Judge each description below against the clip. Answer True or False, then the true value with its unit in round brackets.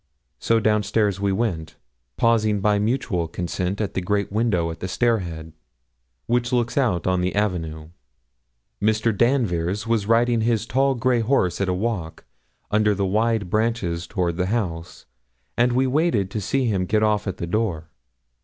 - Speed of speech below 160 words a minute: False (170 wpm)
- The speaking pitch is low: True (105 Hz)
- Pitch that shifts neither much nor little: True (4.2 semitones)